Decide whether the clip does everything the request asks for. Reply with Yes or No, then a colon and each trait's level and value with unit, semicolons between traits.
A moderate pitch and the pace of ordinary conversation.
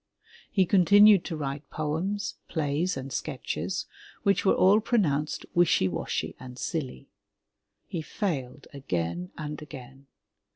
No: medium, 150 Hz; slow, 120 wpm